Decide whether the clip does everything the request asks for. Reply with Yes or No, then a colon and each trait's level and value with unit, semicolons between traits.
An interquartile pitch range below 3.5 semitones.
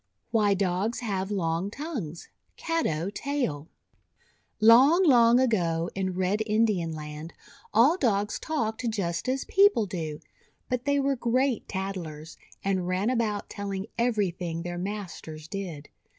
No: average, 5.3 semitones